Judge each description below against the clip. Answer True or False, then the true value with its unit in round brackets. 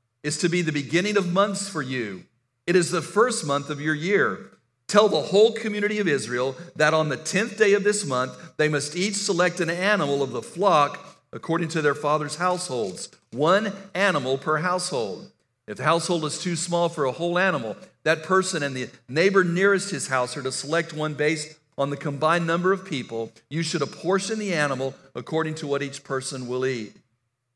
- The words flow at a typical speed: True (195 wpm)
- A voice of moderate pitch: True (155 Hz)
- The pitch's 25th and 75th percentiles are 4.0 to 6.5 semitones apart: True (4.9 semitones)